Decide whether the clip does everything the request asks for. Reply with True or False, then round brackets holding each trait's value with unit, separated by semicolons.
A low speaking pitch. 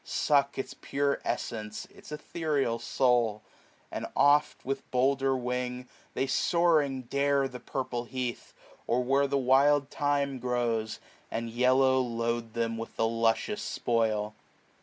True (125 Hz)